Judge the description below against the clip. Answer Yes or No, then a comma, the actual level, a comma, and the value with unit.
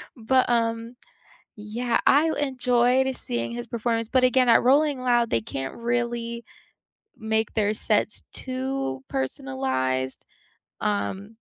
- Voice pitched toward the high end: Yes, high, 230 Hz